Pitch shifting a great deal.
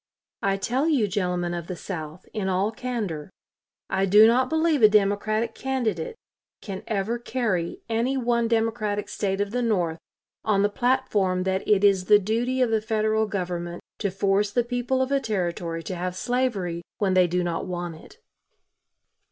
No: average, 4.4 semitones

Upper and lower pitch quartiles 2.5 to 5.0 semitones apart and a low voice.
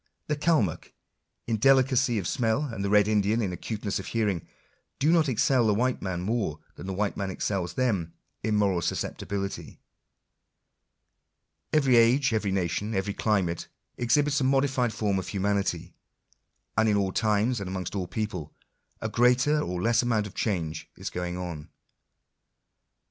Yes: average, 4.2 semitones; low, 105 Hz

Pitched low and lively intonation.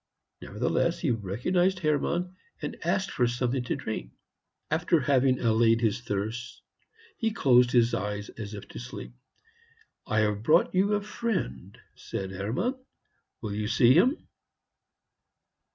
Yes: low, 120 Hz; wide, 7.7 semitones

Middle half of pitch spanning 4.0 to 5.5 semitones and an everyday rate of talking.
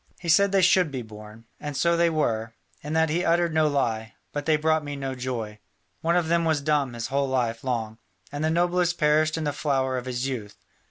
No: average, 4.5 semitones; fast, 225 wpm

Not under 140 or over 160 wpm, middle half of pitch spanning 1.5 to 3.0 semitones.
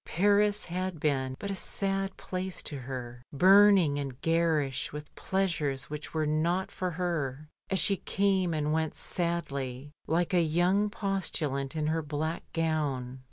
No: average, 150 wpm; average, 4.5 semitones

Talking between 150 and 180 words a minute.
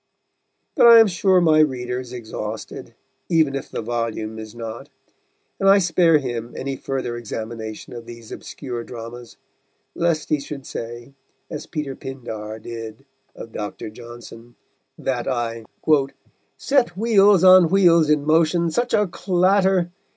No: average, 140 wpm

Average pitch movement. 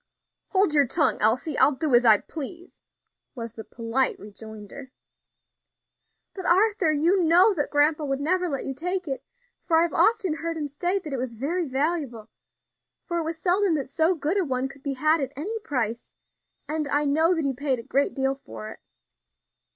Yes: average, 4.3 semitones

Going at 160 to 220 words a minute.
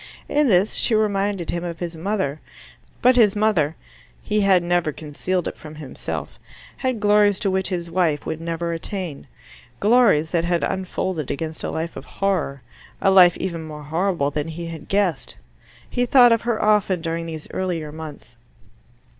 Yes: average, 170 wpm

